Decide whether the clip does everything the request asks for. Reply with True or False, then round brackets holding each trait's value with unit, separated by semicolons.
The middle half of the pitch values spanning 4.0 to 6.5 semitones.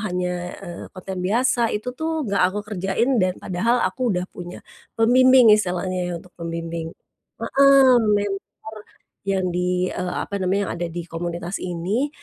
True (4.5 semitones)